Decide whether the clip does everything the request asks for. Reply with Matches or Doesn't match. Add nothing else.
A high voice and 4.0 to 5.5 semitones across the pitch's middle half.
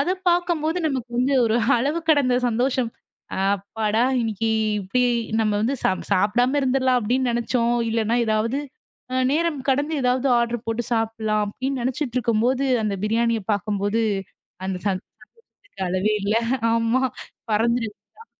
Doesn't match